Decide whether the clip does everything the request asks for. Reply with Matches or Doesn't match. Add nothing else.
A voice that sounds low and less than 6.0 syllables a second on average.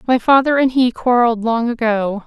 Doesn't match